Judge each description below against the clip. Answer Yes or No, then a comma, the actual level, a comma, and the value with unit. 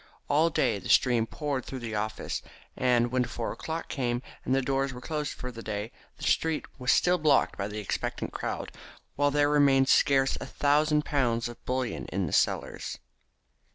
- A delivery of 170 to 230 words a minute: Yes, average, 190 wpm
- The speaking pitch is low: Yes, low, 130 Hz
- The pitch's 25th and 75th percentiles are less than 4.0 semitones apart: Yes, average, 3.5 semitones